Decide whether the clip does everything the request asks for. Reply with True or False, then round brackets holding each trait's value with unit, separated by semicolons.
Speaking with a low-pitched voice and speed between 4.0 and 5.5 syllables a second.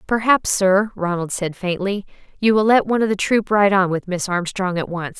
False (195 Hz; 5.1 syllables/s)